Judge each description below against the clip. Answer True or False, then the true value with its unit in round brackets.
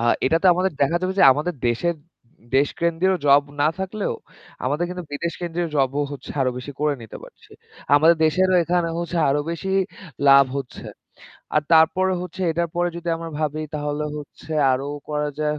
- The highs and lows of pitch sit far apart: False (3.2 semitones)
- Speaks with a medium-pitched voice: True (160 Hz)